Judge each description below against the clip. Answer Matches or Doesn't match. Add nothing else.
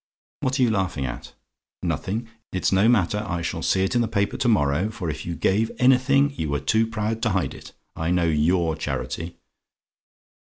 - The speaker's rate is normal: Matches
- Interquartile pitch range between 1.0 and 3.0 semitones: Doesn't match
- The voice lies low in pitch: Matches